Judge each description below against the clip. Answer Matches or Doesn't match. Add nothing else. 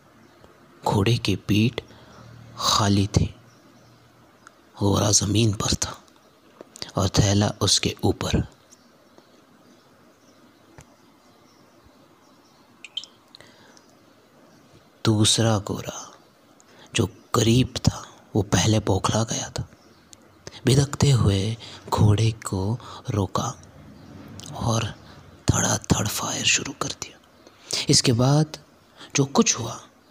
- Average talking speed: Doesn't match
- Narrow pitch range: Doesn't match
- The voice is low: Matches